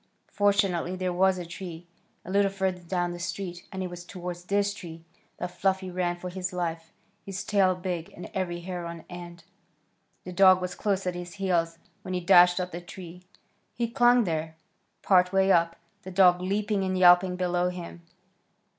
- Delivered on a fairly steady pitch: Yes, narrow, 1.5 semitones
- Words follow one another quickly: No, average, 180 wpm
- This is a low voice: No, medium, 180 Hz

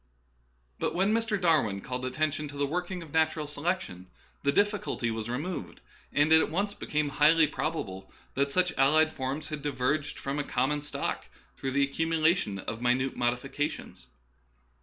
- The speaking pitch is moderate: Yes, medium, 150 Hz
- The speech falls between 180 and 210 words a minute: No, average, 165 wpm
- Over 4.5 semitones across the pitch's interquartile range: No, average, 3.6 semitones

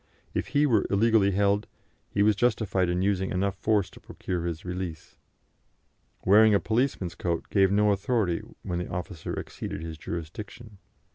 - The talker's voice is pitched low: Yes, low, 100 Hz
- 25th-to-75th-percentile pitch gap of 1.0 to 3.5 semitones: Yes, average, 3.2 semitones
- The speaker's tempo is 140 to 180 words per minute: Yes, average, 155 wpm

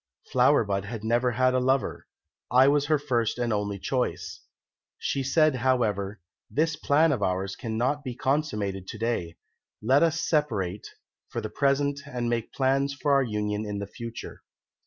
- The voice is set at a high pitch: No, low, 120 Hz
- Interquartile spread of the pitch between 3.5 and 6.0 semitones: Yes, average, 4.9 semitones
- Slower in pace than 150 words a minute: No, average, 165 wpm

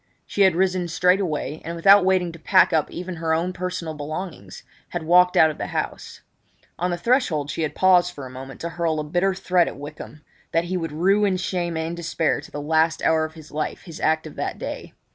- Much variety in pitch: No, narrow, 2.5 semitones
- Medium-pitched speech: Yes, medium, 170 Hz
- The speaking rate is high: Yes, fast, 225 wpm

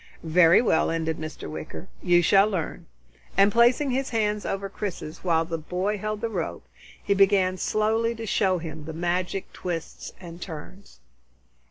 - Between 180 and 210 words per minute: No, average, 160 wpm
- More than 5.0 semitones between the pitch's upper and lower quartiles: No, average, 4.0 semitones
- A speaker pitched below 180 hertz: No, high, 190 Hz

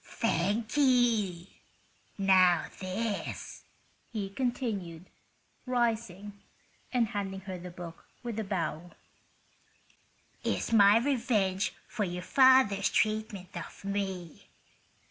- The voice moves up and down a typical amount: Yes, average, 3.8 semitones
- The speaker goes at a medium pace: No, slow, 95 wpm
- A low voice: No, high, 200 Hz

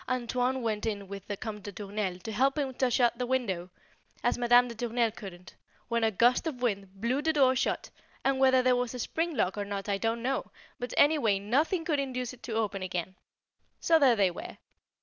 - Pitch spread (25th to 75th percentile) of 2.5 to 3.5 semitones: No, average, 4.2 semitones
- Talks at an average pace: No, fast, 220 wpm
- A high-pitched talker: Yes, high, 235 Hz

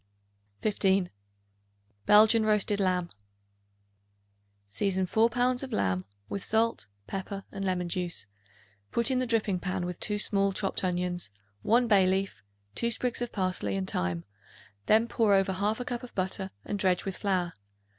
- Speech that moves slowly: No, average, 150 wpm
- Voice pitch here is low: No, high, 195 Hz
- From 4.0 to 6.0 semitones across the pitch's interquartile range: No, average, 3.3 semitones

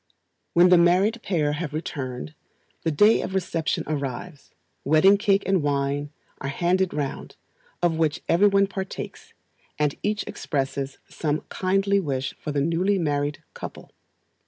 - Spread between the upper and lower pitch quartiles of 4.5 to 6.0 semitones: Yes, average, 4.8 semitones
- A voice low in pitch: No, medium, 165 Hz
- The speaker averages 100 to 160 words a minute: Yes, average, 145 wpm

